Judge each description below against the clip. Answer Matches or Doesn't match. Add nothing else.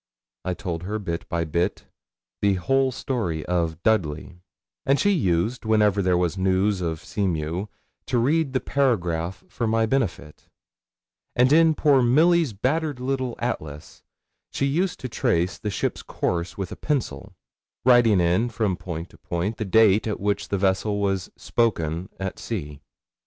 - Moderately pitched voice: Doesn't match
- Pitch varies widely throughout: Matches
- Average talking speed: Matches